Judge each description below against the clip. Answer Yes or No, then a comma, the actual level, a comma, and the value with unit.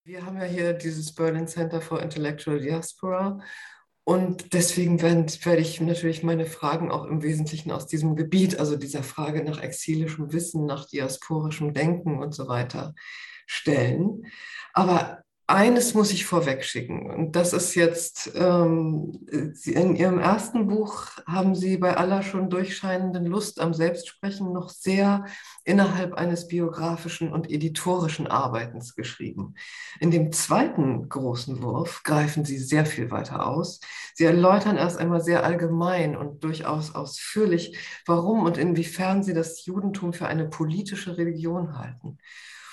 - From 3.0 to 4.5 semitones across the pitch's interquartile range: No, narrow, 2.6 semitones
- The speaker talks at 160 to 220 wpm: No, average, 140 wpm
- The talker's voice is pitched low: No, medium, 170 Hz